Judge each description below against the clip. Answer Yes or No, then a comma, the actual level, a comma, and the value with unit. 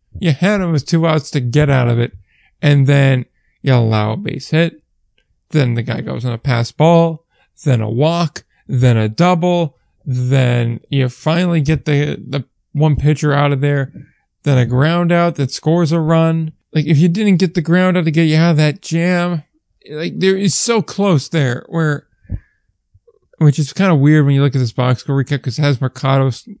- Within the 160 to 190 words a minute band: No, fast, 205 wpm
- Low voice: No, medium, 150 Hz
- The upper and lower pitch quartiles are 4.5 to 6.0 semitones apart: No, average, 4.1 semitones